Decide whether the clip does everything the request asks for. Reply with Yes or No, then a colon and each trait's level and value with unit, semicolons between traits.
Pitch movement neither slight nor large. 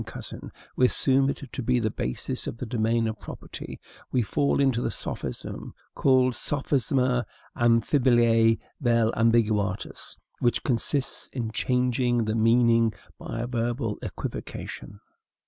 No: narrow, 2.0 semitones